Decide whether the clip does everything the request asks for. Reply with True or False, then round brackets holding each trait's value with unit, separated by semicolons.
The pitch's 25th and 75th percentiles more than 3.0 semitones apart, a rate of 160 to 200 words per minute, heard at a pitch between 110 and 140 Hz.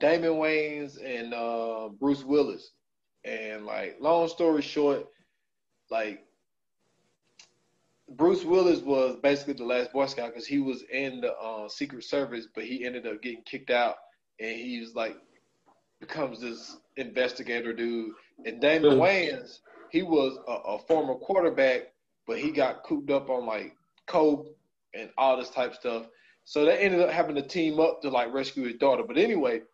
True (4.3 semitones; 165 wpm; 135 Hz)